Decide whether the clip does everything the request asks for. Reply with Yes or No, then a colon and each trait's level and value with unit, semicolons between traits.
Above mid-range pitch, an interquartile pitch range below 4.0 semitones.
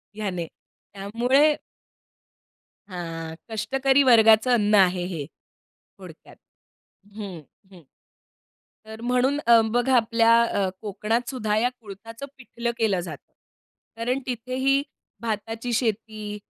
Yes: high, 225 Hz; average, 3.1 semitones